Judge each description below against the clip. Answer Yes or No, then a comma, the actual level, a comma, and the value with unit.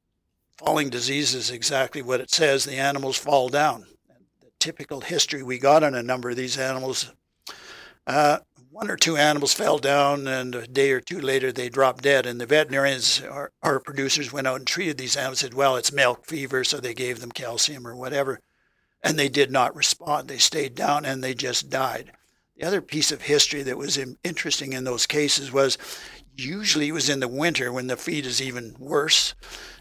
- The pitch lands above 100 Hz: Yes, low, 135 Hz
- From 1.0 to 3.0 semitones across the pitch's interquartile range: Yes, narrow, 2.4 semitones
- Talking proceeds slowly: No, average, 195 wpm